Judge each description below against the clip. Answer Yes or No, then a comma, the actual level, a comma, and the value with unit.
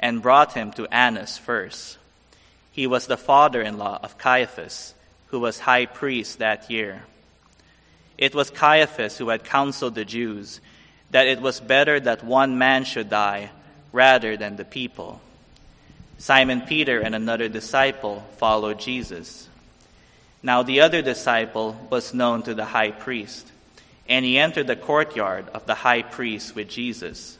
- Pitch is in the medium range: No, low, 120 Hz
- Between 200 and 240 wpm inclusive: No, average, 150 wpm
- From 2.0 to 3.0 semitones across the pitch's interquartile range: No, average, 3.4 semitones